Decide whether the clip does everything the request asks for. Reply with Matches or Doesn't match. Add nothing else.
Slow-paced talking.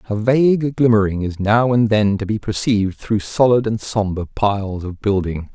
Doesn't match